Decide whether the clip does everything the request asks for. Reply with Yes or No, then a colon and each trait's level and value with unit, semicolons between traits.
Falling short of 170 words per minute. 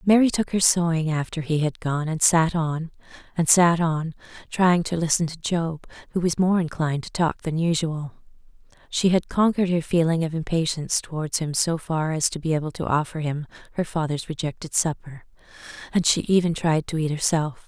No: average, 190 wpm